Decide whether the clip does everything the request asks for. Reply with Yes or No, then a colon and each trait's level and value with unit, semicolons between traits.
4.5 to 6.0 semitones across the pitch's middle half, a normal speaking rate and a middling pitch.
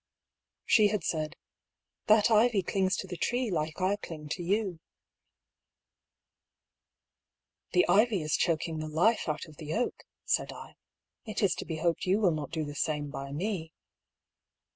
Yes: average, 5.1 semitones; average, 170 wpm; medium, 175 Hz